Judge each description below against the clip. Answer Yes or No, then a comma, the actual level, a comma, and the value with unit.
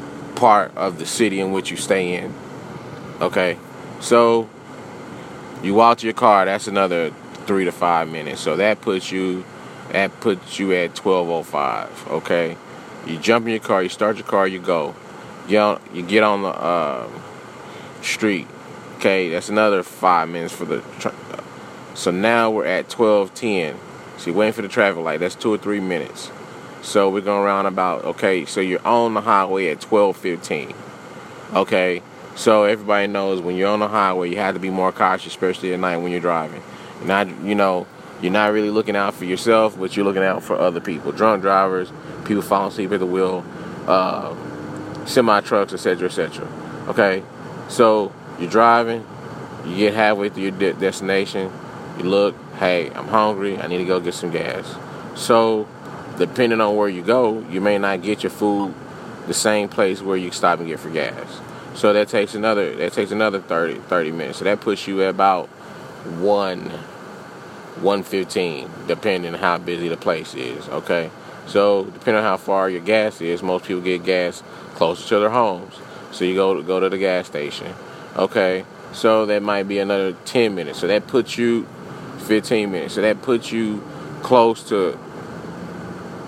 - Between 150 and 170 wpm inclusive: No, average, 180 wpm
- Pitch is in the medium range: No, low, 100 Hz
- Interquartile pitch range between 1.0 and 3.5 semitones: Yes, narrow, 2.6 semitones